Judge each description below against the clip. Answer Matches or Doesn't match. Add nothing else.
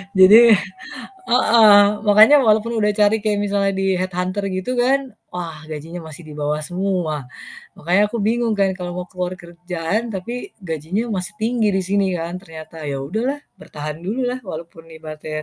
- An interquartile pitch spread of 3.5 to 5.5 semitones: Matches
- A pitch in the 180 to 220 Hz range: Matches